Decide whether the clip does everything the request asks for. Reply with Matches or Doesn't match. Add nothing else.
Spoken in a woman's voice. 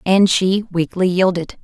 Matches